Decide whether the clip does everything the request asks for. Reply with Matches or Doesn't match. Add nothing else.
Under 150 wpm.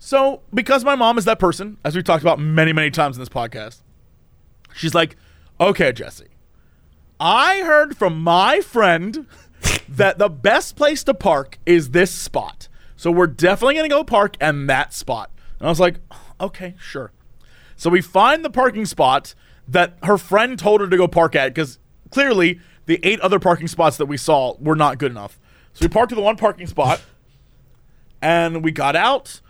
Doesn't match